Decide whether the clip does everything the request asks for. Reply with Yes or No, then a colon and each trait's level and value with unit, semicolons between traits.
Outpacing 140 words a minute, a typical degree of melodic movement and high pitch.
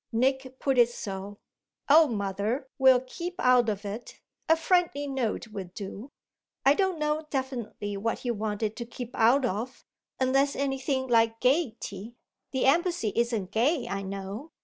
Yes: average, 150 wpm; average, 4.4 semitones; high, 245 Hz